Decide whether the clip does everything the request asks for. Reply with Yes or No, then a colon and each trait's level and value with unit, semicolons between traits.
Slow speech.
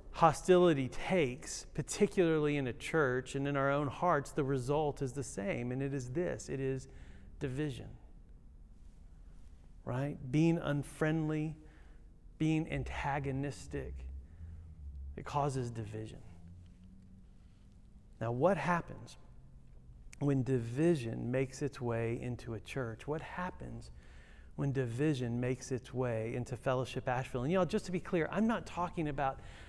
Yes: slow, 125 wpm